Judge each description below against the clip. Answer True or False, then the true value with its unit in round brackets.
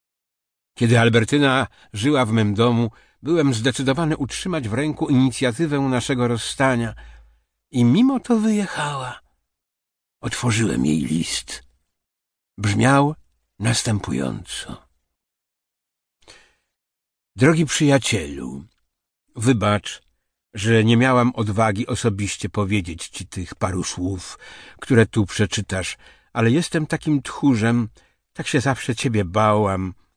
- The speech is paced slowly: True (95 wpm)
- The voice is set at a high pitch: False (120 Hz)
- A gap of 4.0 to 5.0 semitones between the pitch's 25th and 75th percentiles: True (4.7 semitones)